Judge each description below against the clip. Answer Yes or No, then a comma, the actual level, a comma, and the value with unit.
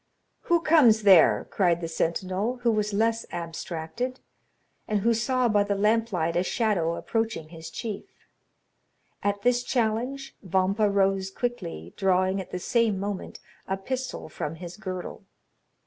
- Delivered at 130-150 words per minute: Yes, average, 145 wpm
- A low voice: No, high, 200 Hz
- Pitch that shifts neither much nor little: Yes, average, 4.0 semitones